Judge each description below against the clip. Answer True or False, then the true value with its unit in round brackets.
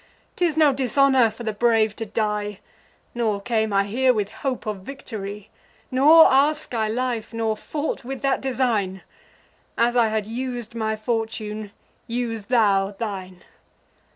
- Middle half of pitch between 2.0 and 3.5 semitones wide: True (3.2 semitones)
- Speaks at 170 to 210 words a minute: False (145 wpm)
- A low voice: False (225 Hz)